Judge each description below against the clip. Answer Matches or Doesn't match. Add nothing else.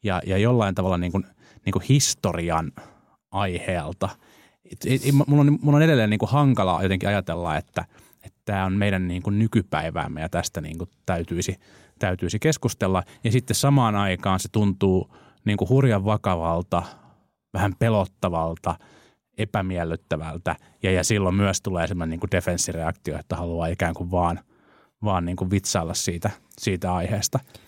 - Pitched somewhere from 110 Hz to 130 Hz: Doesn't match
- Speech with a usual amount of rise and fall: Matches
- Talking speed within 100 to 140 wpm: Doesn't match